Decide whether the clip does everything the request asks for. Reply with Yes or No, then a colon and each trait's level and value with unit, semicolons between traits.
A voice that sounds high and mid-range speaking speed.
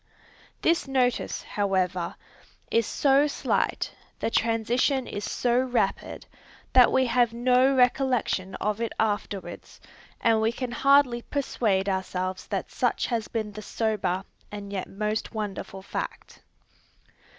No: high, 225 Hz; slow, 125 wpm